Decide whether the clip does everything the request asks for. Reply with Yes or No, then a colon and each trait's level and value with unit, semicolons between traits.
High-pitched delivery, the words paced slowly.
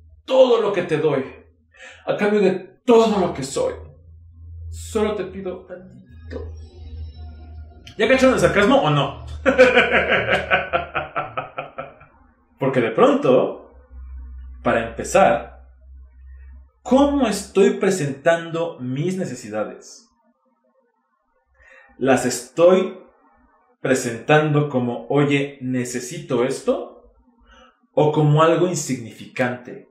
No: low, 135 Hz; slow, 85 wpm